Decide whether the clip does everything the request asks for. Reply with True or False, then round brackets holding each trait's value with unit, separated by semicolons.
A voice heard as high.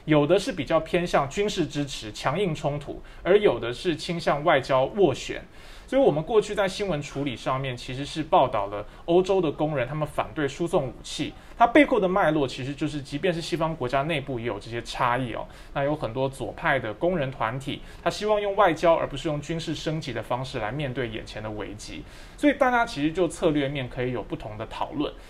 False (150 Hz)